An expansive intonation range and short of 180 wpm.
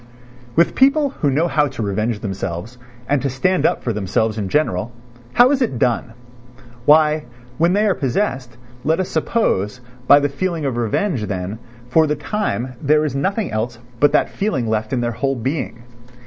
No: wide, 6.1 semitones; average, 185 wpm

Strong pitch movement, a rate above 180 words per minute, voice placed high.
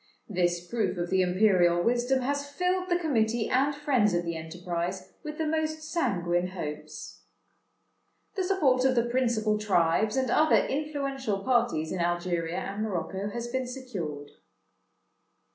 No: wide, 7.4 semitones; average, 145 wpm; high, 220 Hz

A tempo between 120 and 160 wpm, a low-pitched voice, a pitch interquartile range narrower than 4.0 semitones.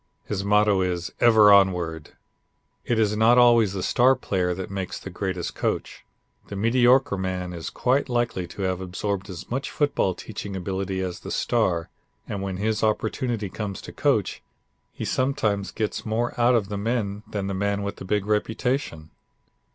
No: average, 170 wpm; low, 100 Hz; average, 3.3 semitones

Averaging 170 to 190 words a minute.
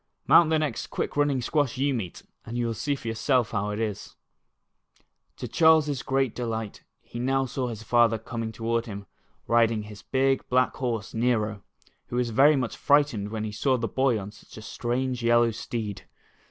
Yes: average, 185 wpm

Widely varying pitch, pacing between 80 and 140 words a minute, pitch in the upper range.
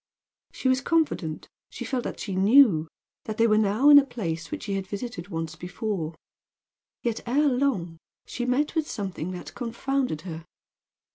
No: wide, 6.7 semitones; average, 165 wpm; high, 215 Hz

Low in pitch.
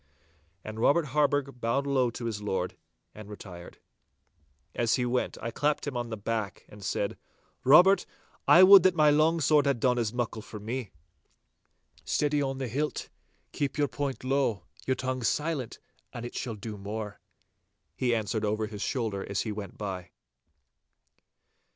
Yes: low, 120 Hz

